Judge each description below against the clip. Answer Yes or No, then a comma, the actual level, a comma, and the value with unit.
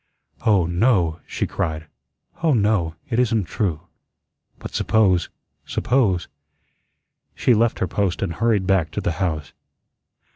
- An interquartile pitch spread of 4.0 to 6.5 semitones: Yes, average, 4.6 semitones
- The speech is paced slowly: Yes, slow, 130 wpm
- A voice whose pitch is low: Yes, very low, 95 Hz